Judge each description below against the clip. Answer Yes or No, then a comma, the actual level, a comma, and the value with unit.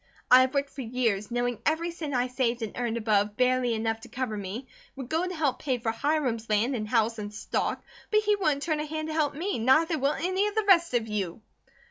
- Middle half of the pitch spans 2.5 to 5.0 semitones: No, wide, 5.6 semitones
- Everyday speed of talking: No, fast, 235 wpm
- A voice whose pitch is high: Yes, very high, 255 Hz